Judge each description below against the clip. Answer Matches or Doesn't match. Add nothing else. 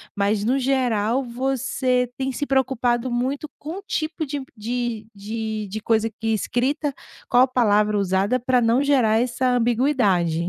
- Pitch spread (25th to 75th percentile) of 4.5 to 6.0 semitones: Doesn't match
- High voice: Matches